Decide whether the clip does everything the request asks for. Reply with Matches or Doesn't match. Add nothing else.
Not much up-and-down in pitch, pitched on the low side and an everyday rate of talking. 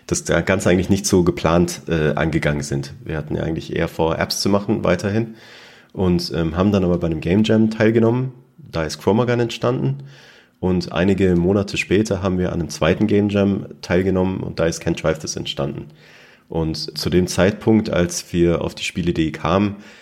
Doesn't match